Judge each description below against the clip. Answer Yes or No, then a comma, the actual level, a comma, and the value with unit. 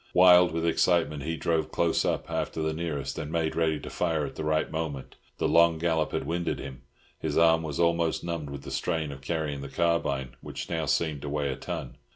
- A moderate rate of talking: No, fast, 215 wpm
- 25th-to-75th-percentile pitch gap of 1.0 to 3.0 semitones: Yes, narrow, 2.4 semitones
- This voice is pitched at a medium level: No, very low, 80 Hz